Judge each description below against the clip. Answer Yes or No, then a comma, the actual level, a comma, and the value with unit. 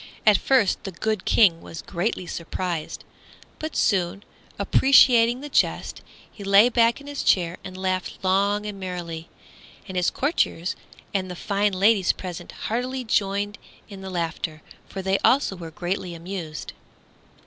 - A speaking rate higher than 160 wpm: No, average, 150 wpm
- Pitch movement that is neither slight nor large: Yes, average, 3.4 semitones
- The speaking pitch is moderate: No, high, 195 Hz